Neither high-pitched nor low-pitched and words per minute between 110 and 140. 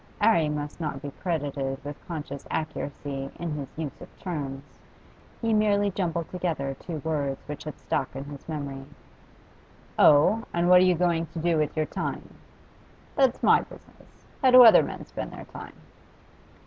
No: medium, 155 Hz; average, 165 wpm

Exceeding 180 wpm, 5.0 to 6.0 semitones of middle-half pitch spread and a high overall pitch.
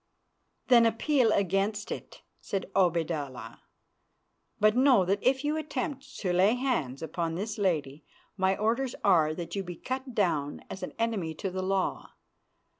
No: average, 150 wpm; wide, 5.4 semitones; high, 195 Hz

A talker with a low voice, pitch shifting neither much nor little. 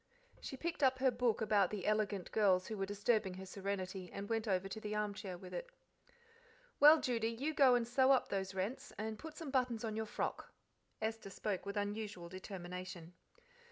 No: high, 210 Hz; average, 3.8 semitones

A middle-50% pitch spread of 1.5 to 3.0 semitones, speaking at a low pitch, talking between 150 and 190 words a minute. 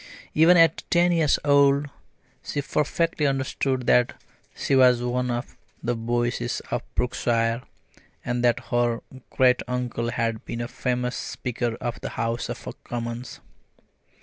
No: narrow, 2.5 semitones; low, 125 Hz; slow, 135 wpm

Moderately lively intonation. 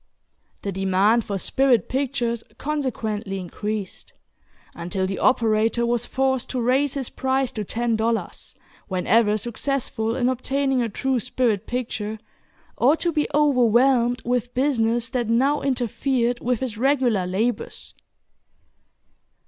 Yes: average, 3.3 semitones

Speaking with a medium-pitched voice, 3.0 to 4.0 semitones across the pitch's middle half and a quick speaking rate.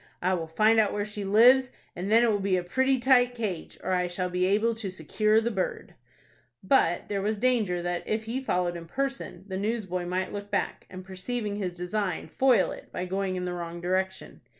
No: high, 195 Hz; average, 3.6 semitones; fast, 215 wpm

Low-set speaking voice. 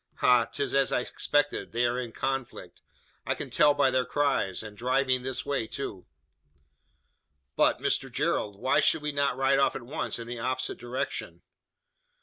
Yes: low, 130 Hz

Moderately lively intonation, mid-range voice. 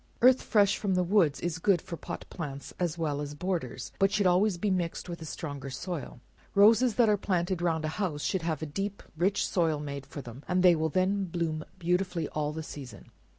Yes: average, 4.0 semitones; medium, 170 Hz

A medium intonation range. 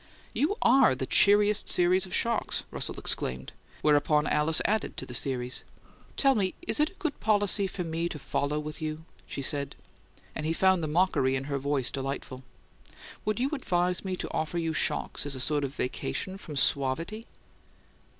No: wide, 5.8 semitones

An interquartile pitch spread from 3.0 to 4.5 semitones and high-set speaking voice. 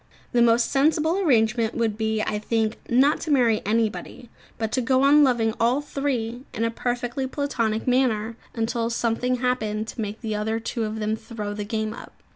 No: narrow, 2.6 semitones; high, 230 Hz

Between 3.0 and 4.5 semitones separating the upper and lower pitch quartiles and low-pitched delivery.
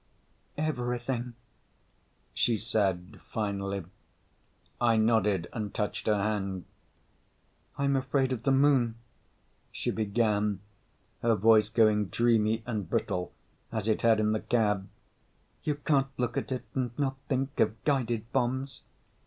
Yes: average, 3.3 semitones; low, 115 Hz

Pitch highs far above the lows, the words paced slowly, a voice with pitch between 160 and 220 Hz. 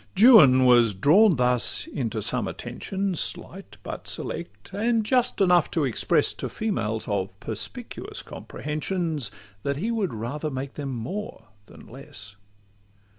No: wide, 8.6 semitones; slow, 130 wpm; medium, 145 Hz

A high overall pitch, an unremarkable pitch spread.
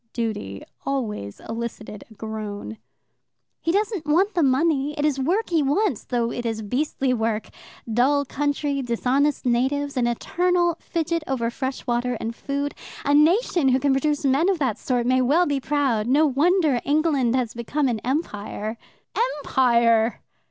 Yes: very high, 270 Hz; average, 4.1 semitones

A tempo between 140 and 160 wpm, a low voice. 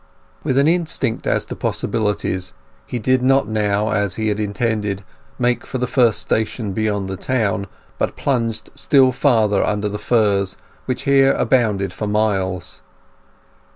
Yes: average, 150 wpm; low, 110 Hz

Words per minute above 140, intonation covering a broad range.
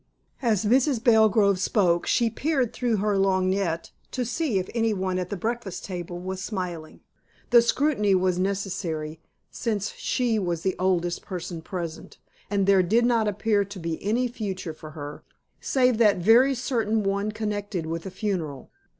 No: average, 160 wpm; average, 3.8 semitones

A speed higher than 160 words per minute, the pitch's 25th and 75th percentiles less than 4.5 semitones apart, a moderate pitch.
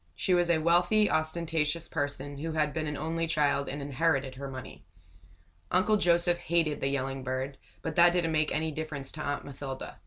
Yes: average, 185 wpm; average, 3.1 semitones; medium, 155 Hz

